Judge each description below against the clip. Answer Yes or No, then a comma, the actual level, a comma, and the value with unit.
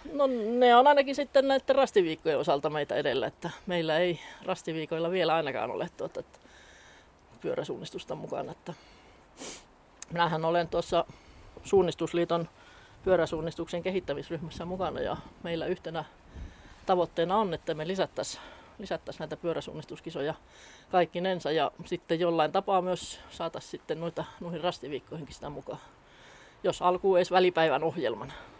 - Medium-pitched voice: Yes, medium, 175 Hz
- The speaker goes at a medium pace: Yes, average, 120 wpm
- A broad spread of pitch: No, average, 2.7 semitones